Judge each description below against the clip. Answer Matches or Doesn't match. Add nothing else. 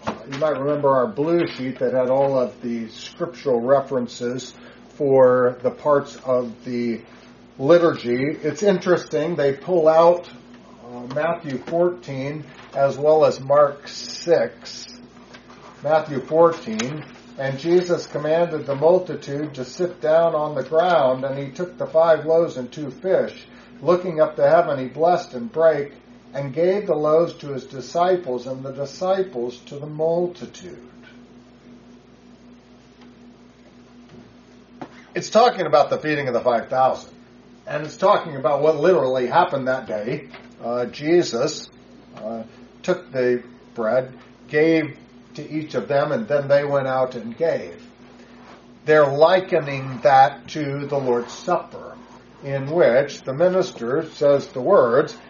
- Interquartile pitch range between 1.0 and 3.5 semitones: Doesn't match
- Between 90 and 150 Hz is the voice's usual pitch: Matches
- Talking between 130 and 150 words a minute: Matches